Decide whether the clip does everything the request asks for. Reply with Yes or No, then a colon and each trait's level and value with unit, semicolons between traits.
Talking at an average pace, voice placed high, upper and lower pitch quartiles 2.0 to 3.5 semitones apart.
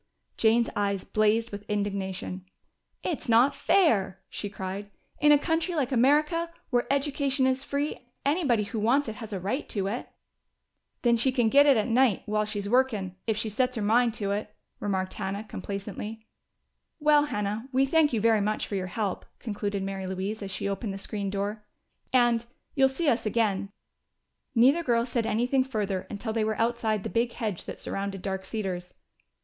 No: average, 180 wpm; high, 220 Hz; average, 4.4 semitones